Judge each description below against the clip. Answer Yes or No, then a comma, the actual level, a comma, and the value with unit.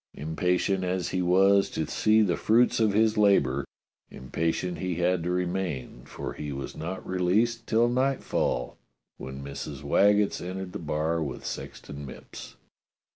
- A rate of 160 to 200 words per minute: No, average, 150 wpm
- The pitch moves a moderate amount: Yes, average, 4.8 semitones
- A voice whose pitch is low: Yes, very low, 90 Hz